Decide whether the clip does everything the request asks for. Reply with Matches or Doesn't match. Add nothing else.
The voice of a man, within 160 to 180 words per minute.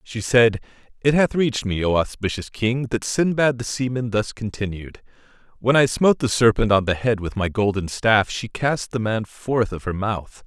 Doesn't match